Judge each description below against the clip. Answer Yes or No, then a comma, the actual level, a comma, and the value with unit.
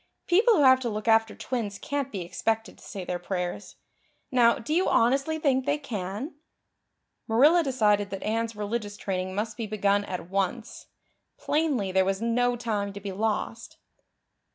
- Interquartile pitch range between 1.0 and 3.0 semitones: No, average, 4.4 semitones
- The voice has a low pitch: No, high, 225 Hz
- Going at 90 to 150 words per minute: No, average, 165 wpm